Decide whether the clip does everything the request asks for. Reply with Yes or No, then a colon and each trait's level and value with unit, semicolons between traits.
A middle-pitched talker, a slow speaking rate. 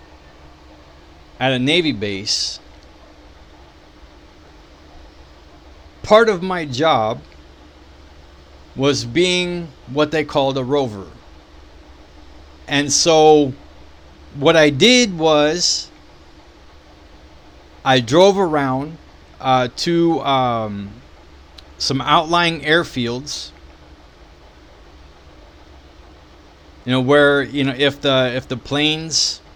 No: very low, 80 Hz; slow, 80 wpm